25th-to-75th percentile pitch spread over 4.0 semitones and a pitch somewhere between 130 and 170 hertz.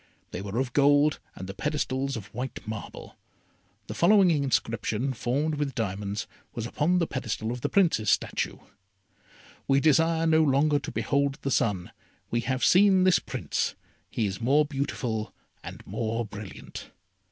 Yes: average, 5.1 semitones; low, 135 Hz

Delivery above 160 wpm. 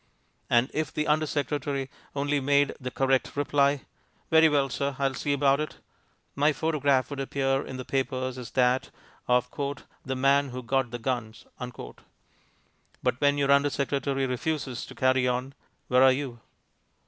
No: average, 155 wpm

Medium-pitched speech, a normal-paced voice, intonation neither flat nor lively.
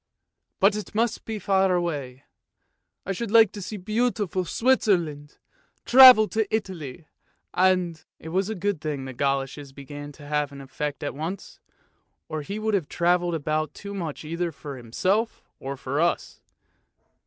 No: medium, 175 Hz; average, 165 wpm; wide, 5.7 semitones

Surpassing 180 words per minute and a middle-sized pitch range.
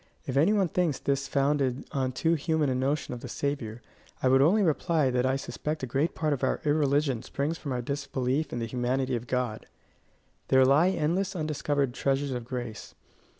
Yes: average, 195 wpm; average, 3.0 semitones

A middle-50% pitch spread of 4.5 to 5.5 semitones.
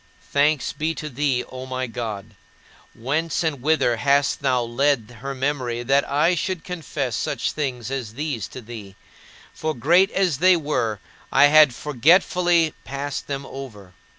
No: average, 4.1 semitones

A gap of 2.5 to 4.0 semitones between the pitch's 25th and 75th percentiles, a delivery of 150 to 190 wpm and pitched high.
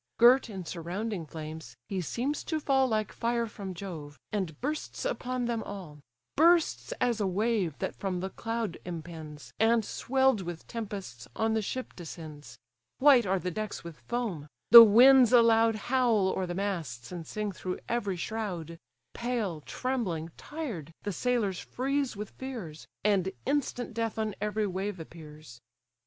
No: wide, 5.6 semitones; average, 155 wpm; high, 205 Hz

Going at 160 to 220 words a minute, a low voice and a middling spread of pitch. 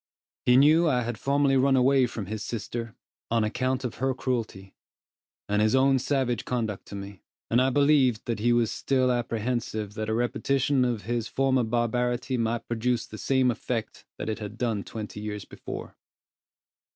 Yes: average, 175 wpm; low, 120 Hz; average, 3.0 semitones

